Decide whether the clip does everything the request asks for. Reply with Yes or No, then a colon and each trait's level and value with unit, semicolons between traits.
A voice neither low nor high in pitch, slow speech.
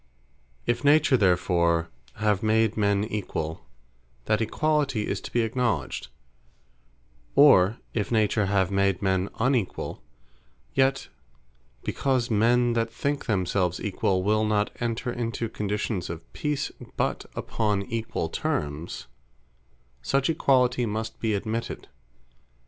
No: low, 110 Hz; slow, 115 wpm